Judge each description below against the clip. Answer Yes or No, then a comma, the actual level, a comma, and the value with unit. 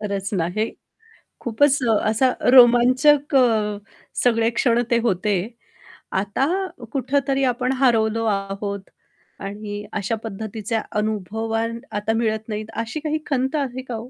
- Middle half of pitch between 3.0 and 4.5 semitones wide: Yes, average, 3.3 semitones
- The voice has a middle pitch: No, high, 225 Hz